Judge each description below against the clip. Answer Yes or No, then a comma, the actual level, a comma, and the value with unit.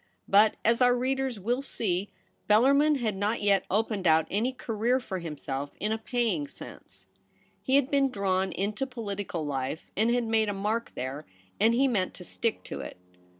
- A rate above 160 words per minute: Yes, average, 180 wpm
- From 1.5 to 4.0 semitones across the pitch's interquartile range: No, average, 4.4 semitones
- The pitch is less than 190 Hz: No, high, 215 Hz